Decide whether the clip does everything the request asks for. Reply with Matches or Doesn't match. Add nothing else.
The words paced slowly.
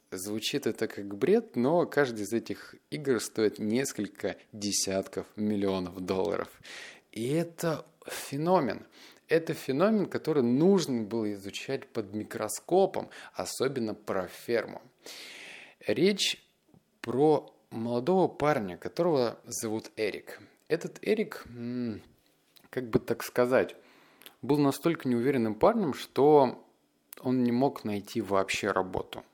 Matches